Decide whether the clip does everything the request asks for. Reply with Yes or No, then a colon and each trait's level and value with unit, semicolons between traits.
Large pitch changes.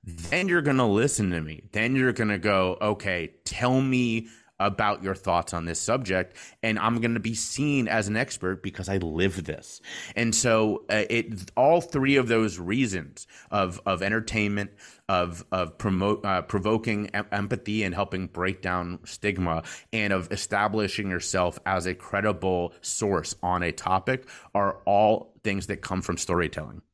No: average, 3.3 semitones